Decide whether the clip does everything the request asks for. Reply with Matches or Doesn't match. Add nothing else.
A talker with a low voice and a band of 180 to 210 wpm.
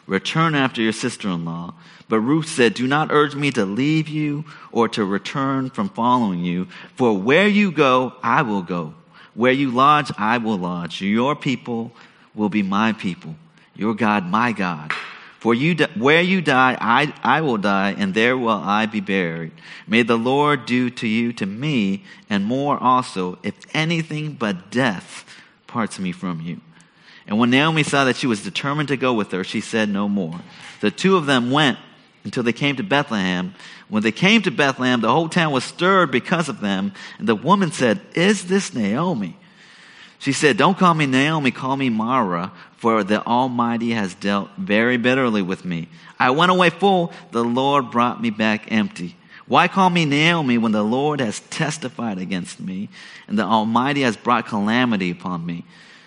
Matches